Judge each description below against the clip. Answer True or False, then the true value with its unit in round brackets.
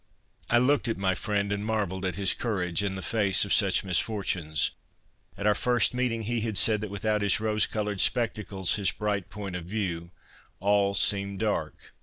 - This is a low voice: True (100 Hz)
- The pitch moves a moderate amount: False (2.1 semitones)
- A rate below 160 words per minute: False (185 wpm)